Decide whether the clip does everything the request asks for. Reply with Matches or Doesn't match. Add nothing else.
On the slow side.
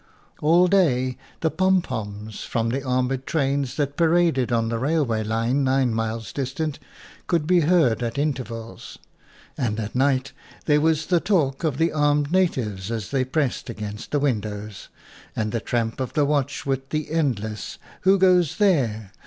Doesn't match